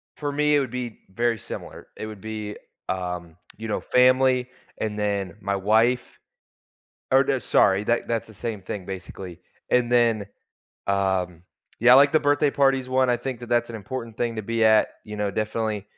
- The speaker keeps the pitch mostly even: No, average, 3.7 semitones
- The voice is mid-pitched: No, low, 115 Hz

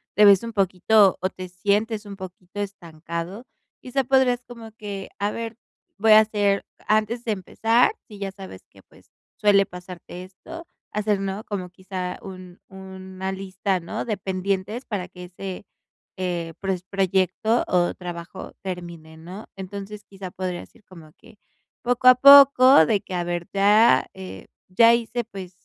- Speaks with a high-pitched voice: Yes, high, 195 Hz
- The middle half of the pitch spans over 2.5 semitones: Yes, average, 2.9 semitones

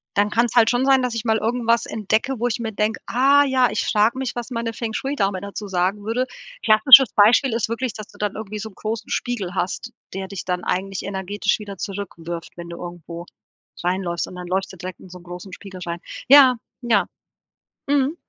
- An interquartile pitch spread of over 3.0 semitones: Yes, average, 4.1 semitones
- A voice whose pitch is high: Yes, high, 215 Hz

